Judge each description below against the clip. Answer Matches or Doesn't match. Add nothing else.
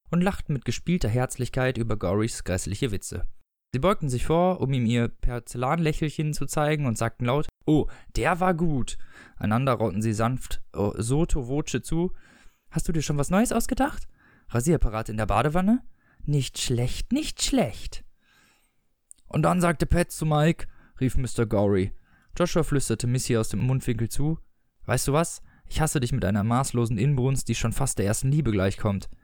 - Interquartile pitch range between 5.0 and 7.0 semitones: Matches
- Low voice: Matches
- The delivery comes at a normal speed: Matches